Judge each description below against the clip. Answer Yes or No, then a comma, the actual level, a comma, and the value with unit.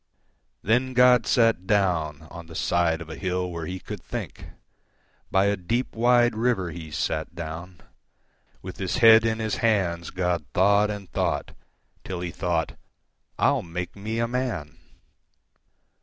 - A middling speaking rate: No, slow, 130 wpm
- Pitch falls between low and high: No, very low, 95 Hz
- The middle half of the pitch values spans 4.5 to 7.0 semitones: Yes, average, 4.8 semitones